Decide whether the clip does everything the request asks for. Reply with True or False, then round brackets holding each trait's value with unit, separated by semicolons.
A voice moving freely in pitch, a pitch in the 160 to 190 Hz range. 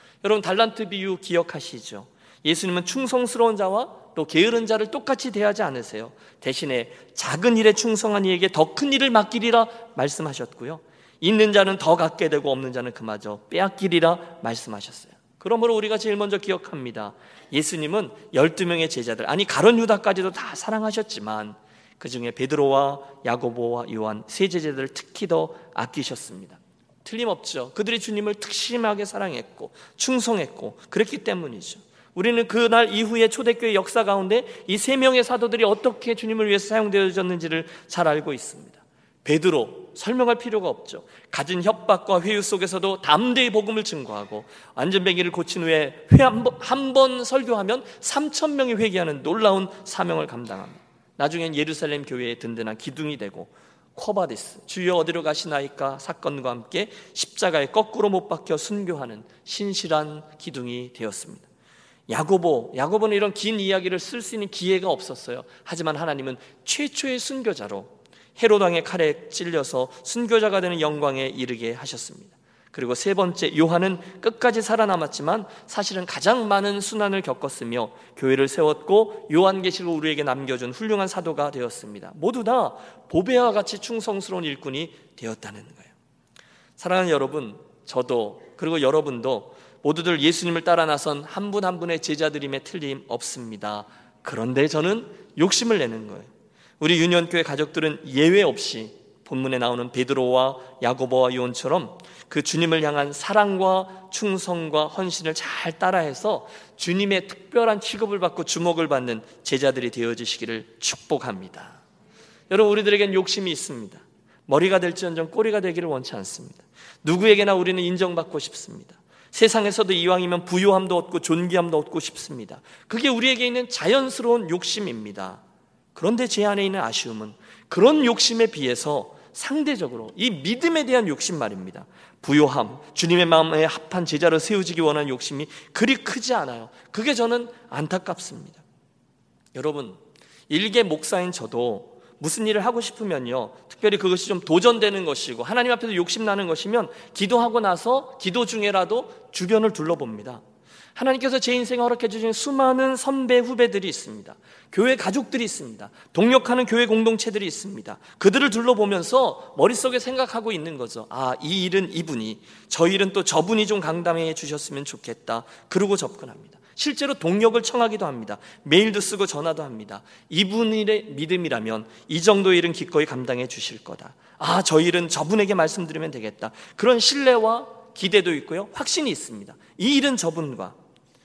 True (6.9 semitones; 185 Hz)